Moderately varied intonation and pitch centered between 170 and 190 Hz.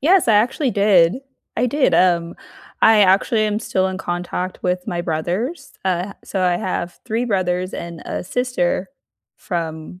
Yes: average, 3.9 semitones; medium, 185 Hz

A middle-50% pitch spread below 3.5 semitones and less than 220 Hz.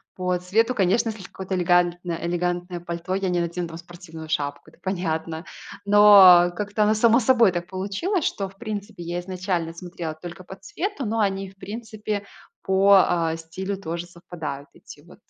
Yes: average, 2.9 semitones; medium, 185 Hz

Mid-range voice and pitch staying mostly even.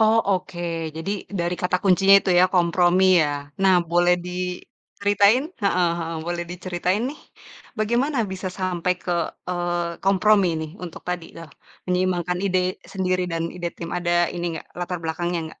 Yes: medium, 180 Hz; narrow, 1.5 semitones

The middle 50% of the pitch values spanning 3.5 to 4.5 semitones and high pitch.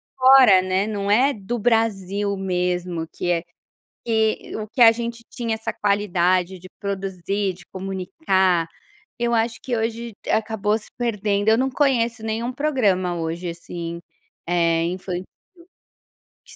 Yes: average, 3.9 semitones; high, 205 Hz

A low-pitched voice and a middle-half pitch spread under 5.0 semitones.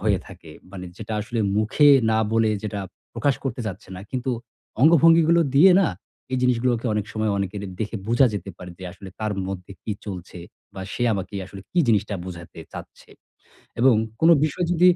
No: low, 110 Hz; wide, 5.4 semitones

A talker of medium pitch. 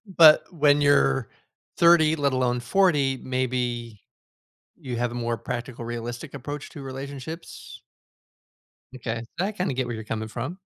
No: low, 130 Hz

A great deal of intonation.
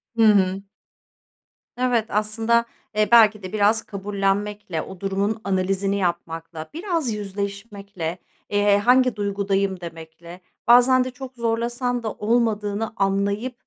No: average, 3.0 semitones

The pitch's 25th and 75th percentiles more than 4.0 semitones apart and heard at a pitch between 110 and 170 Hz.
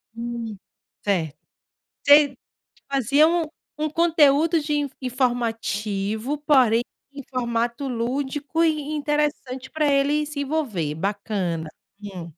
No: average, 4.7 semitones; very high, 265 Hz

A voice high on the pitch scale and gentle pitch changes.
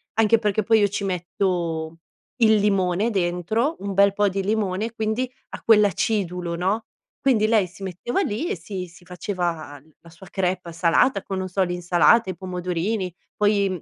No: high, 195 Hz; average, 3.2 semitones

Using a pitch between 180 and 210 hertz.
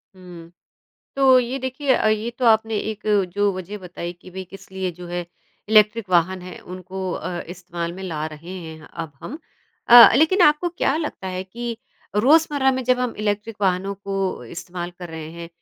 Yes: high, 190 Hz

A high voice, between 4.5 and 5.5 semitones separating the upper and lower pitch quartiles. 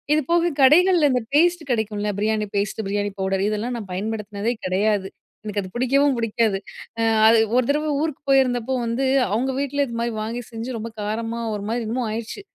No: high, 230 Hz; average, 4.0 semitones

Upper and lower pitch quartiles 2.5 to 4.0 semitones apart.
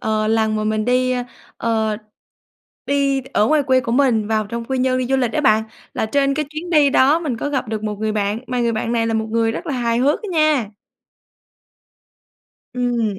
Yes: average, 3.7 semitones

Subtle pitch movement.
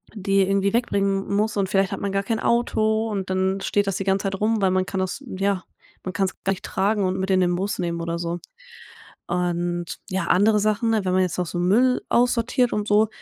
Yes: narrow, 2.3 semitones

